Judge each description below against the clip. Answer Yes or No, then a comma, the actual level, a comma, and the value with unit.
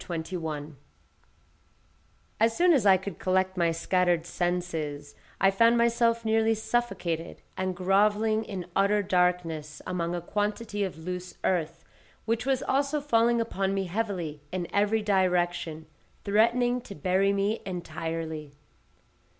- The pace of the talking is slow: Yes, slow, 130 wpm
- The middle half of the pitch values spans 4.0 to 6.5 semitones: Yes, average, 4.3 semitones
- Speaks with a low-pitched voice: No, high, 190 Hz